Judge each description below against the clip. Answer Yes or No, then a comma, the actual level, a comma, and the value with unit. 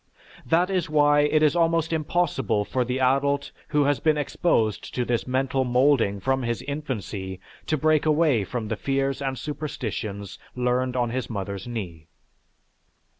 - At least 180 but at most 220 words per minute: No, average, 155 wpm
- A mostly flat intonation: No, average, 4.1 semitones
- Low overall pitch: Yes, low, 130 Hz